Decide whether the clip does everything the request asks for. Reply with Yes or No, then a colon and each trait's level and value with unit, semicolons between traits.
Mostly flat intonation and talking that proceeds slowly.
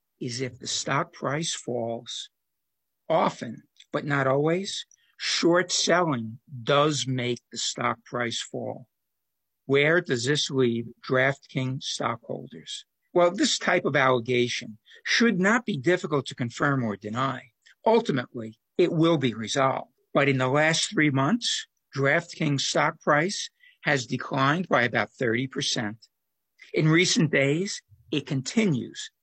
No: average, 5.0 semitones; slow, 125 wpm